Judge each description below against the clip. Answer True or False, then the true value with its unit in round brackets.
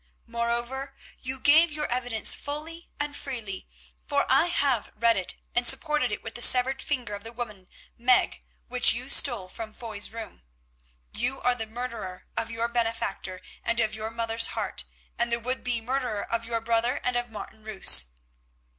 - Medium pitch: False (235 Hz)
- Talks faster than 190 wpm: False (175 wpm)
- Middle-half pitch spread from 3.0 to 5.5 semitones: False (2.4 semitones)